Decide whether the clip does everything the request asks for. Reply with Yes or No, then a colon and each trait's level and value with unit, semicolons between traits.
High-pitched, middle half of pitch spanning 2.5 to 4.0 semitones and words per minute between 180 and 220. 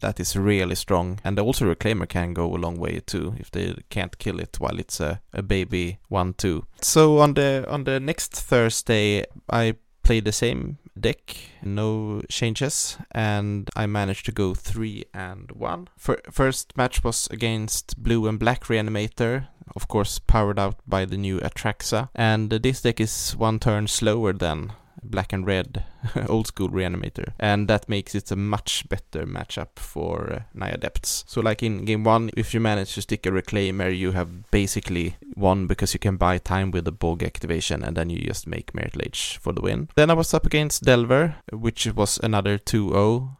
No: low, 105 Hz; average, 3.6 semitones; average, 185 wpm